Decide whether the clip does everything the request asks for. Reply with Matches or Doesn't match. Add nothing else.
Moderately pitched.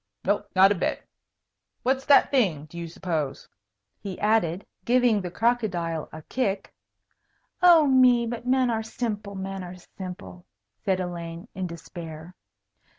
Doesn't match